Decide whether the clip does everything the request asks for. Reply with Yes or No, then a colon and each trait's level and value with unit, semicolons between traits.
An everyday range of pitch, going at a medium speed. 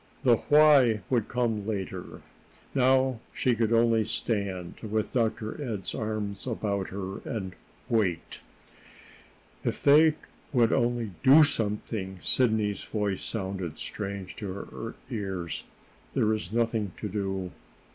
No: average, 3.1 semitones; slow, 120 wpm